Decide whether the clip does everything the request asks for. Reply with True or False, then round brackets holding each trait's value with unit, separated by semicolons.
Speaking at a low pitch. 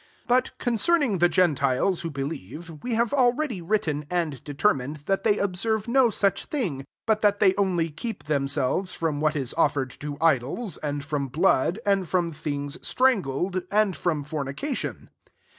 False (170 Hz)